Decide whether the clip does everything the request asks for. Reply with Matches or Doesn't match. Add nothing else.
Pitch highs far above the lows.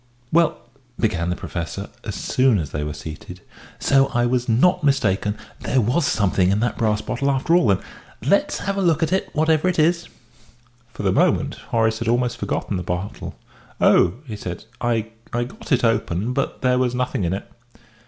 Matches